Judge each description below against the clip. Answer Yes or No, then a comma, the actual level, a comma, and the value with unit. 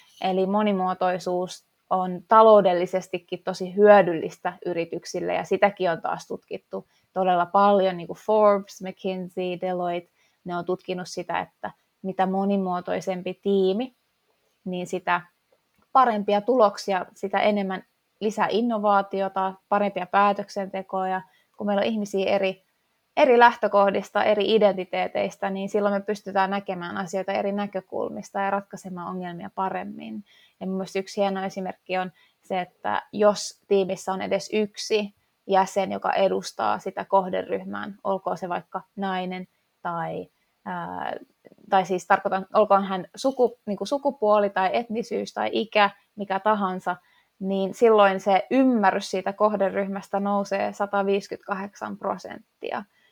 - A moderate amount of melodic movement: No, narrow, 1.6 semitones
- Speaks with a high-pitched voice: Yes, high, 195 Hz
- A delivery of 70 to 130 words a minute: Yes, average, 120 wpm